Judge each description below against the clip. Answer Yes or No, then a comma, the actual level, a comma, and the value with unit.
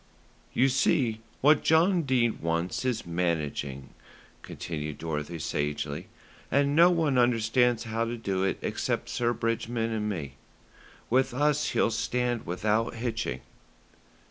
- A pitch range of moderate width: No, wide, 6.8 semitones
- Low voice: Yes, low, 115 Hz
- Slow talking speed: Yes, slow, 125 wpm